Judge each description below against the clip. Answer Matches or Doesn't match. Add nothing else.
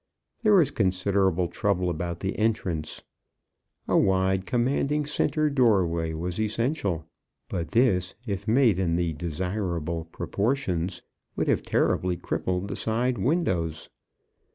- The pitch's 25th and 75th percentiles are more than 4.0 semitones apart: Matches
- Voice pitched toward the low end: Matches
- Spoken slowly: Matches